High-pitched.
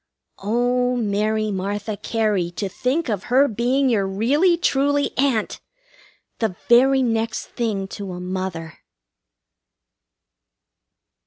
Yes: high, 225 Hz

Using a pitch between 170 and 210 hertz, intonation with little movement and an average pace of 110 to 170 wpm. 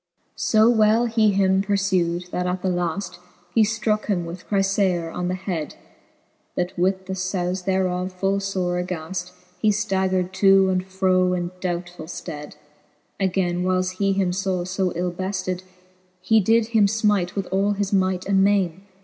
Yes: high, 190 Hz; narrow, 1.7 semitones; average, 165 wpm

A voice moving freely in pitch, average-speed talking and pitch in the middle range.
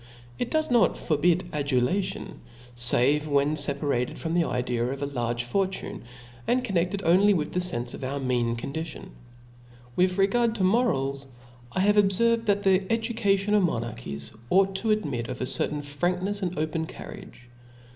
Yes: wide, 6.4 semitones; average, 160 wpm; medium, 170 Hz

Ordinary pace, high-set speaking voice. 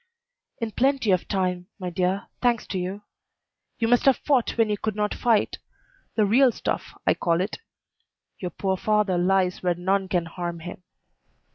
Yes: average, 170 wpm; high, 195 Hz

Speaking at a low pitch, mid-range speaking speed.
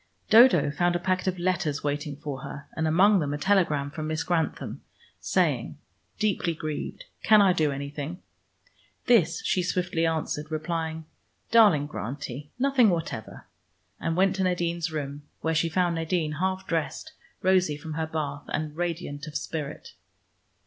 No: medium, 165 Hz; average, 150 wpm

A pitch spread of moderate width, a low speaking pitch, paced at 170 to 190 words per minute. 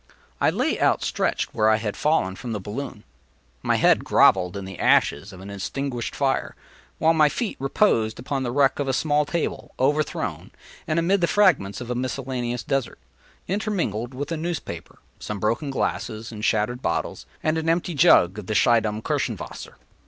No: wide, 6.1 semitones; low, 125 Hz; average, 175 wpm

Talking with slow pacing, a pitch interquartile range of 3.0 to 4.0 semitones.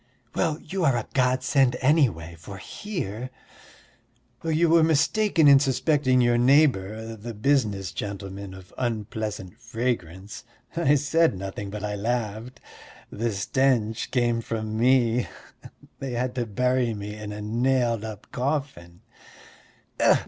No: slow, 125 wpm; average, 4.4 semitones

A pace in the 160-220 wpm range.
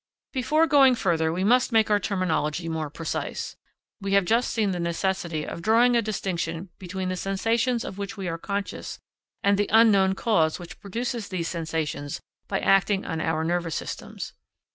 Yes: average, 170 wpm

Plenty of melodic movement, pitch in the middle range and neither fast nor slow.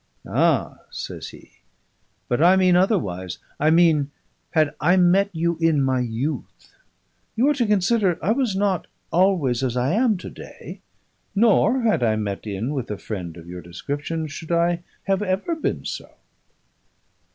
Yes: wide, 7.5 semitones; medium, 165 Hz; average, 160 wpm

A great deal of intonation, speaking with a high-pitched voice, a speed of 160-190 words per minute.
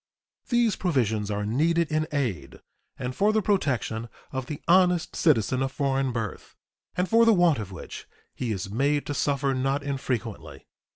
No: wide, 6.3 semitones; low, 135 Hz; average, 165 wpm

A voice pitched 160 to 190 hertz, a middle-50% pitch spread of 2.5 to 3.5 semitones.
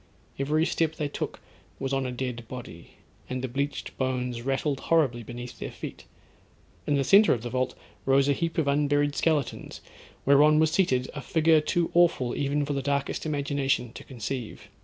No: medium, 140 Hz; average, 2.9 semitones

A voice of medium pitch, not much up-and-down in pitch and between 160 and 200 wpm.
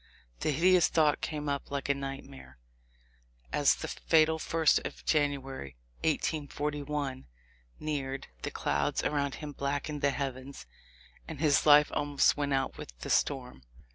No: medium, 145 Hz; narrow, 1.7 semitones; average, 140 wpm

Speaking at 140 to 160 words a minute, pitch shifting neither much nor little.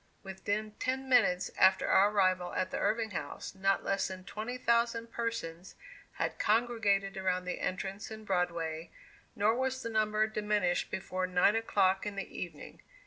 Yes: average, 155 wpm; average, 3.2 semitones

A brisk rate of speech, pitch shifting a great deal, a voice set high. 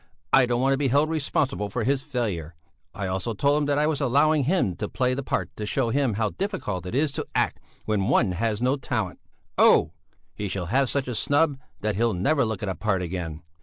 No: fast, 230 wpm; wide, 5.7 semitones; low, 125 Hz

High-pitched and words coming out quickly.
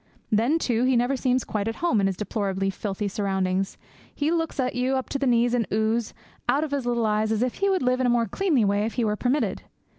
Yes: high, 235 Hz; fast, 250 wpm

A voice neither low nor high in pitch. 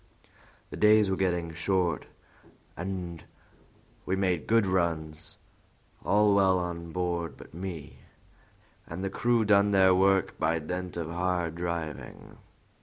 No: very low, 90 Hz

